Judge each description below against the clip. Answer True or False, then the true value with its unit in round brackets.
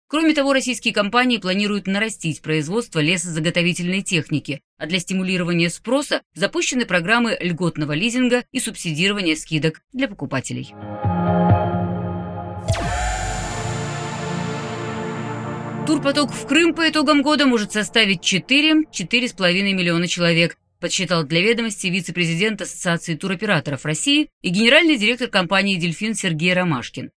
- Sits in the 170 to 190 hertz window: True (185 Hz)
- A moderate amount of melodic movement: False (6.9 semitones)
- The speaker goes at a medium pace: False (105 wpm)